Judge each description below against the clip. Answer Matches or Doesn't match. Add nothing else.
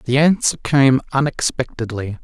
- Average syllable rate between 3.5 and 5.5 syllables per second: Matches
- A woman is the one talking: Doesn't match